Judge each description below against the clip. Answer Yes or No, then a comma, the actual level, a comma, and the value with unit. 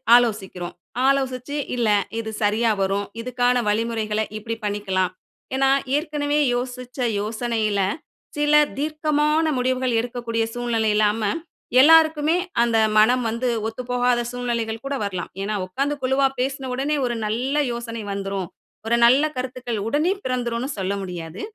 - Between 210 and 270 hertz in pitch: Yes, high, 240 Hz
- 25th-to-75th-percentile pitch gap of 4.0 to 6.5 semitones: No, average, 3.4 semitones